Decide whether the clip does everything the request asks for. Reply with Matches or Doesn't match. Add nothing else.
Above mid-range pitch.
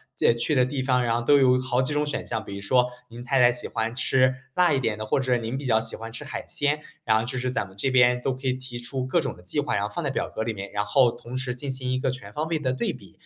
Doesn't match